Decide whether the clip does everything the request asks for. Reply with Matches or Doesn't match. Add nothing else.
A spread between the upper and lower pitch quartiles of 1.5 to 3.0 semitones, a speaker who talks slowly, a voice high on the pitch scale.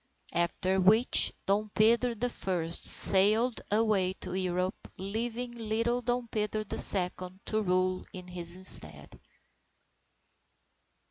Doesn't match